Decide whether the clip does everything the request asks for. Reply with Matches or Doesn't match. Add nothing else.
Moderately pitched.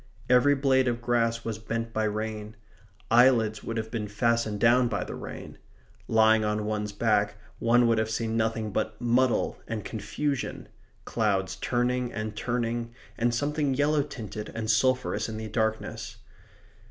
Doesn't match